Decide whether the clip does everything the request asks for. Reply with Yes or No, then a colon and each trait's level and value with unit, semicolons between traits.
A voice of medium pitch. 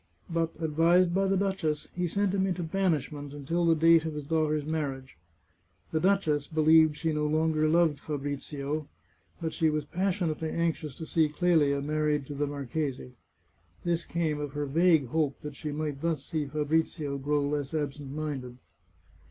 Yes: medium, 155 Hz